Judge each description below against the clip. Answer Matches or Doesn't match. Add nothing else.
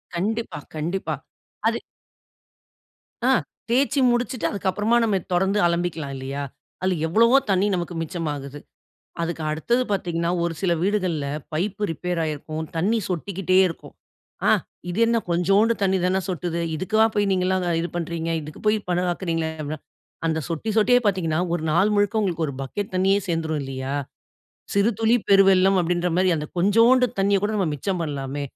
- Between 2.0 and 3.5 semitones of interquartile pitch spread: Doesn't match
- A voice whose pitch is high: Doesn't match